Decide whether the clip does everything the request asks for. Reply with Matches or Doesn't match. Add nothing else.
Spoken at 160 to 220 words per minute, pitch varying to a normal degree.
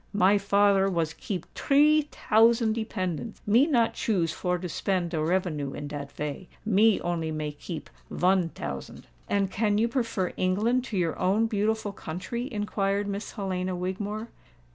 Doesn't match